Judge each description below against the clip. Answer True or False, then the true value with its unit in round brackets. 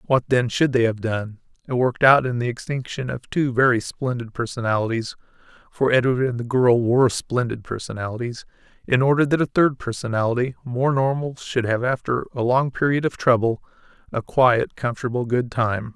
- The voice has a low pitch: True (125 Hz)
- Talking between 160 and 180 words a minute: True (165 wpm)